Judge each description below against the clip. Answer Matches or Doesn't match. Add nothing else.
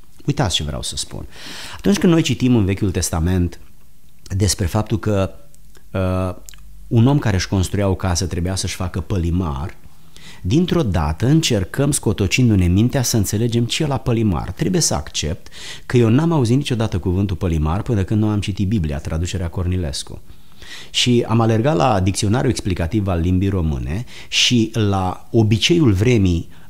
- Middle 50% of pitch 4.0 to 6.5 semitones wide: Matches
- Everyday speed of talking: Matches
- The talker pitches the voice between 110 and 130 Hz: Doesn't match